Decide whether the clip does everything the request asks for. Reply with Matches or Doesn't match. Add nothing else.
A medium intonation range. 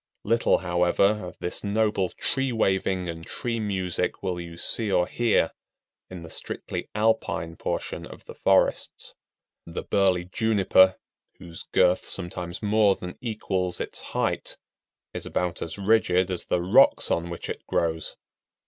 Matches